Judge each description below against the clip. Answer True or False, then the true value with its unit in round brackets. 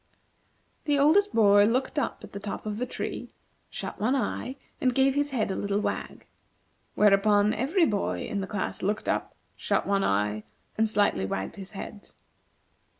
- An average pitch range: True (4.6 semitones)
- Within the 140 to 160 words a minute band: False (170 wpm)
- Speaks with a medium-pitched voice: False (210 Hz)